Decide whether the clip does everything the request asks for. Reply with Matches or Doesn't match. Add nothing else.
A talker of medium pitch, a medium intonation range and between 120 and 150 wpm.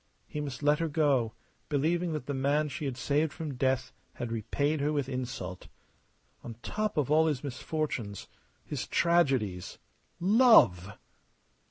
Matches